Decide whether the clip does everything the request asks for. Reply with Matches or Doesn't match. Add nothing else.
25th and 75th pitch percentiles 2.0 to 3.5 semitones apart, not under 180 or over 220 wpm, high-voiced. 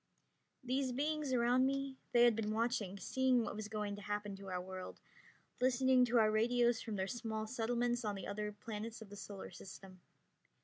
Matches